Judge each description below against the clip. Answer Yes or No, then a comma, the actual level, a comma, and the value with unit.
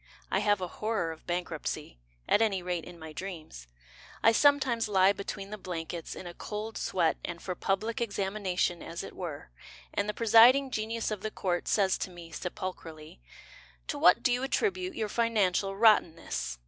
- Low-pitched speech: No, high, 195 Hz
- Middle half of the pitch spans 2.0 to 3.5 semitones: No, average, 3.9 semitones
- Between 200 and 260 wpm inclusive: No, average, 175 wpm